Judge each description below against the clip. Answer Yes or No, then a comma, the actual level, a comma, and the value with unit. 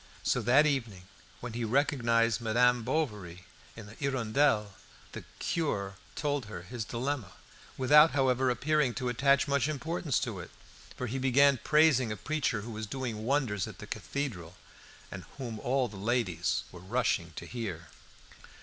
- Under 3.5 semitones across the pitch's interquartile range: No, average, 4.5 semitones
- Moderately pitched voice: No, low, 125 Hz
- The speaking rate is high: No, average, 155 wpm